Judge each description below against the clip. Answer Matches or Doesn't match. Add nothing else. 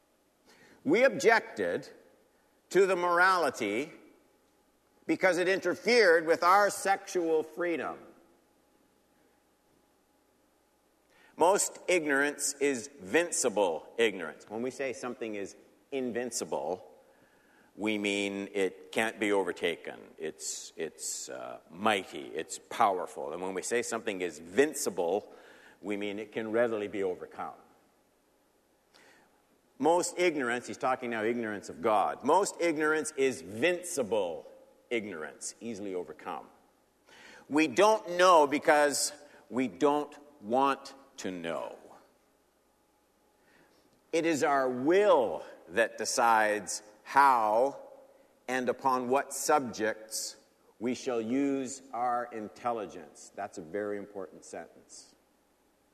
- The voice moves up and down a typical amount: Doesn't match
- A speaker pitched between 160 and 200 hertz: Doesn't match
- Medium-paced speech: Doesn't match